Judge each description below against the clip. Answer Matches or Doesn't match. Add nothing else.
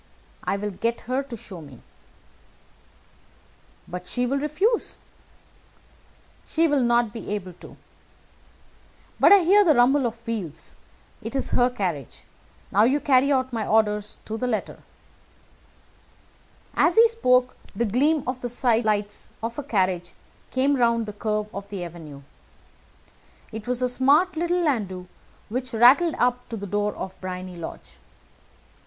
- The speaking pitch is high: Matches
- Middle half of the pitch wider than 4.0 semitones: Matches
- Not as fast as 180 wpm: Matches